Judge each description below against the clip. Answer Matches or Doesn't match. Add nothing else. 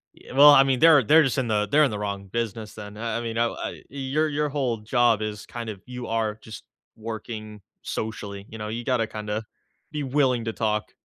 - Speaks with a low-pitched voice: Matches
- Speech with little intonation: Doesn't match